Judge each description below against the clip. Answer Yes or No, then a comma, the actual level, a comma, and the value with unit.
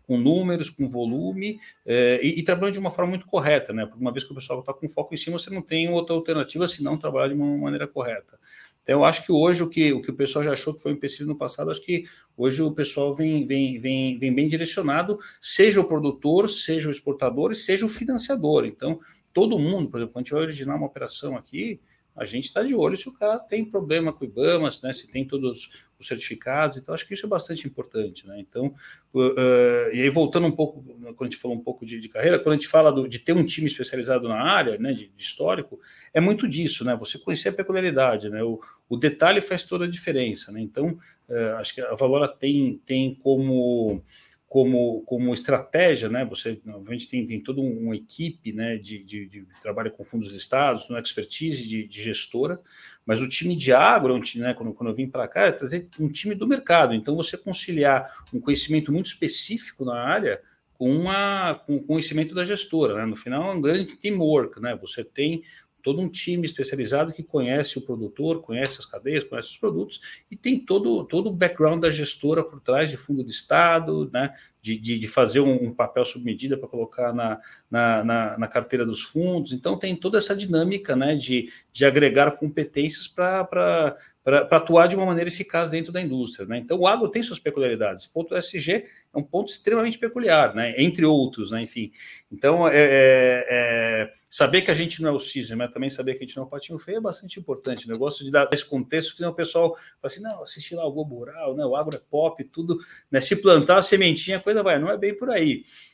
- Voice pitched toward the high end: No, medium, 145 Hz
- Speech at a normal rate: No, fast, 225 wpm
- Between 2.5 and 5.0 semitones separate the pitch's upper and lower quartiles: No, wide, 5.4 semitones